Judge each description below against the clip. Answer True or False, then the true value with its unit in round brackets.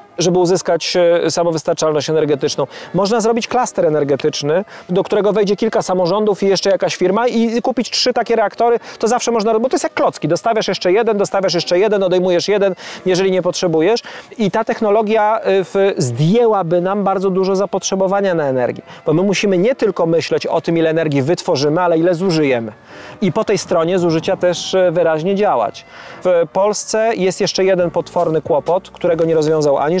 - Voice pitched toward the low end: False (185 Hz)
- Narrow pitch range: False (3.5 semitones)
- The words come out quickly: True (170 wpm)